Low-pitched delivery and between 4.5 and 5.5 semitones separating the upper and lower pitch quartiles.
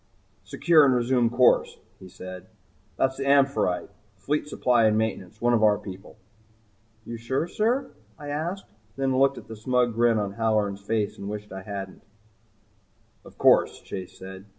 Yes: low, 115 Hz; average, 4.8 semitones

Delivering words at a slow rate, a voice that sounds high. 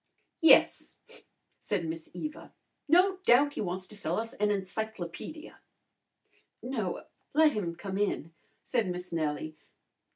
Yes: slow, 120 wpm; high, 205 Hz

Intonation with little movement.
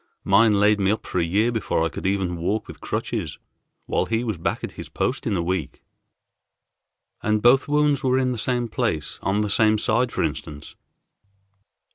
No: average, 4.7 semitones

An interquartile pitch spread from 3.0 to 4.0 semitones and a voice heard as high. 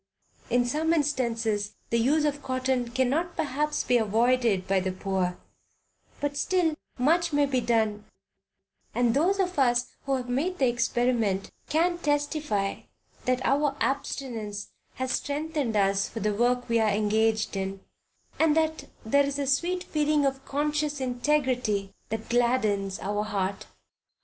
No: average, 5.1 semitones; very high, 250 Hz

